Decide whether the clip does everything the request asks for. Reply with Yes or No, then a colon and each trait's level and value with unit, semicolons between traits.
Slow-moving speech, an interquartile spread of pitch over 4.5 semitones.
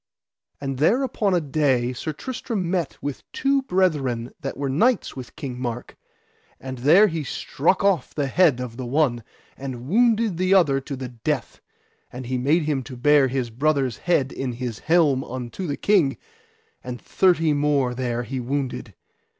No: average, 170 wpm; average, 5.3 semitones